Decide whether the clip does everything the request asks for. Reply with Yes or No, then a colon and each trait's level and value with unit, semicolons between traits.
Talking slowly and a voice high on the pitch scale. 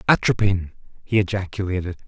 No: slow, 85 wpm; very low, 95 Hz